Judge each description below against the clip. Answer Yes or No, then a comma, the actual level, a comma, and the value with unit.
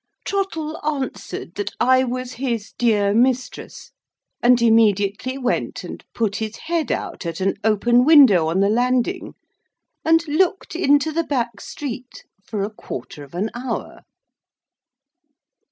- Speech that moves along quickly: No, slow, 135 wpm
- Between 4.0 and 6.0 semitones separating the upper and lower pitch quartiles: Yes, average, 5.1 semitones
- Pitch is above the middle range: Yes, high, 245 Hz